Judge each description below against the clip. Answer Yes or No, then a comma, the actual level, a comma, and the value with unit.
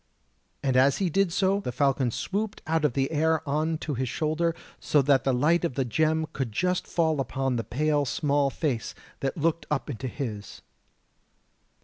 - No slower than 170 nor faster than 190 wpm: Yes, average, 175 wpm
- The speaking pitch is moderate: Yes, medium, 145 Hz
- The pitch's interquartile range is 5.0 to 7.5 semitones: No, average, 3.3 semitones